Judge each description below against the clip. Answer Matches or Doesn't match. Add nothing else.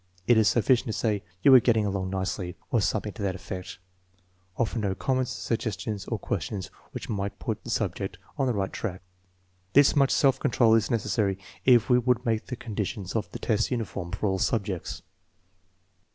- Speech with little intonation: Doesn't match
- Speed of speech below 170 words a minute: Doesn't match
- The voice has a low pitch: Matches